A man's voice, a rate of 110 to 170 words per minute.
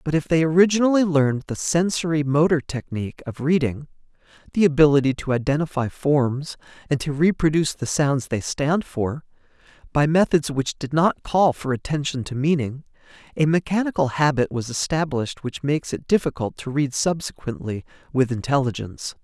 Yes: male; average, 145 wpm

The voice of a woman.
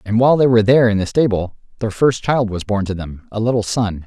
No: male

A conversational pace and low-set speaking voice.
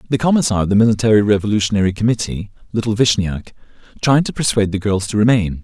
Yes: average, 170 wpm; low, 110 Hz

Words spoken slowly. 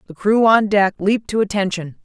No: fast, 205 wpm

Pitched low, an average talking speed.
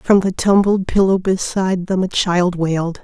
No: medium, 185 Hz; average, 180 wpm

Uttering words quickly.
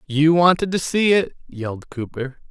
No: average, 165 wpm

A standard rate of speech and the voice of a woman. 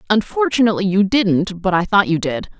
Yes: average, 185 wpm; female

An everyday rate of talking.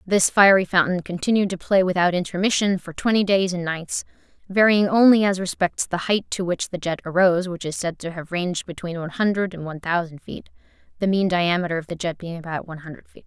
No: fast, 215 wpm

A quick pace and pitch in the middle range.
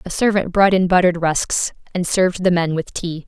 Yes: fast, 220 wpm; medium, 180 Hz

